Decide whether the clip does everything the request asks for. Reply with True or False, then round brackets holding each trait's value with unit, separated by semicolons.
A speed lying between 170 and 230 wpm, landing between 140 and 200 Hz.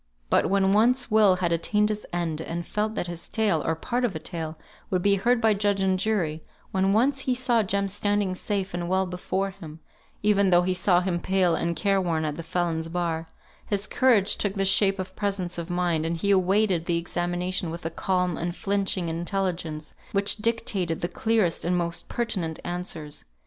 True (195 wpm; 185 Hz)